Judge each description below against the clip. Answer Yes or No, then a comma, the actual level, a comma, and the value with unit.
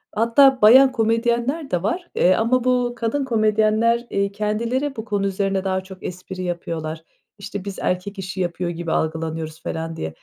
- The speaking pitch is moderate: No, high, 205 Hz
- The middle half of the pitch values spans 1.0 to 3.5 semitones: No, average, 4.6 semitones